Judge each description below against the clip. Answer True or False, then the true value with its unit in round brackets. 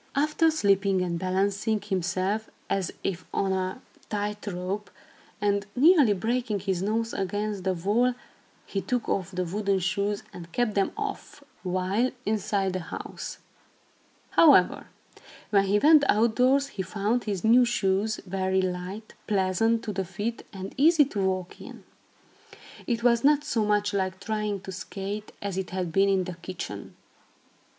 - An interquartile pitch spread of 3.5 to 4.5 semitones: False (3.0 semitones)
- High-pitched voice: True (200 Hz)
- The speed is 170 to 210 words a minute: False (150 wpm)